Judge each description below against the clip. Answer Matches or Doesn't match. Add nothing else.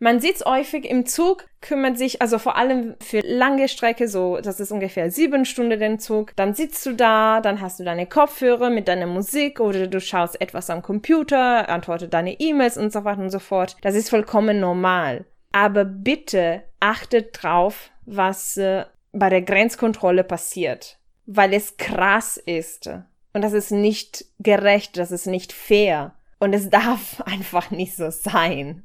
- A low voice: Doesn't match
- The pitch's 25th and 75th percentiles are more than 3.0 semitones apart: Matches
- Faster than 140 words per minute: Matches